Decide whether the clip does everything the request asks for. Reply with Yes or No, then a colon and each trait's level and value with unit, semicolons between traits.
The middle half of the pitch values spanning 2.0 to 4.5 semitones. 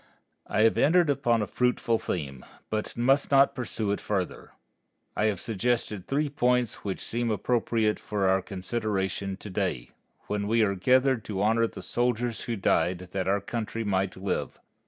Yes: average, 3.8 semitones